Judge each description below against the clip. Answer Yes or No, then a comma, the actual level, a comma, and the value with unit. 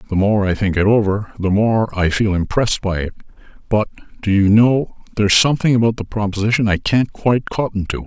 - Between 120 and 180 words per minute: No, average, 200 wpm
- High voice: No, low, 105 Hz